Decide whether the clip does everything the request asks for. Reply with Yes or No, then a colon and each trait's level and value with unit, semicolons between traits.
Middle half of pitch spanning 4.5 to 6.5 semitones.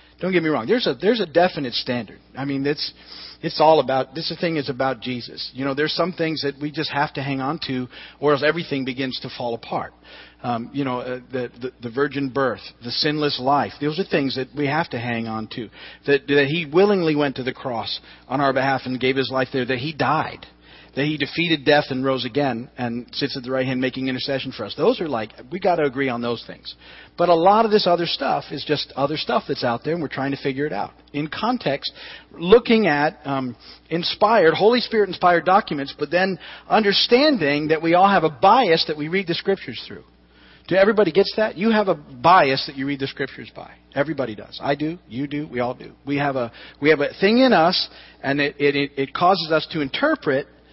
No: average, 4.1 semitones